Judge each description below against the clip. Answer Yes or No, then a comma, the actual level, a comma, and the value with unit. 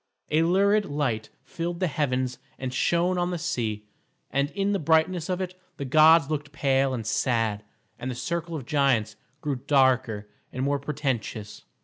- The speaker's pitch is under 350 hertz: Yes, medium, 140 Hz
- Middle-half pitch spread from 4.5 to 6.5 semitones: Yes, average, 4.8 semitones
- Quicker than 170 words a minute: No, average, 165 wpm